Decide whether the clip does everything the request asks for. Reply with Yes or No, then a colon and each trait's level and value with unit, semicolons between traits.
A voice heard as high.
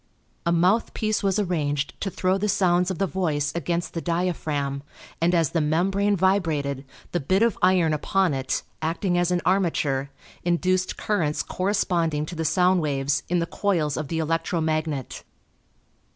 No: medium, 170 Hz